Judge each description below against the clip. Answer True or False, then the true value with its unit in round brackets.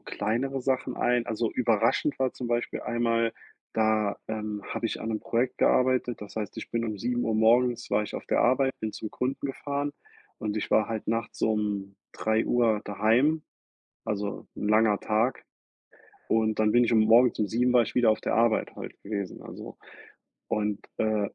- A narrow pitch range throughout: True (2.3 semitones)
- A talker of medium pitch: False (115 Hz)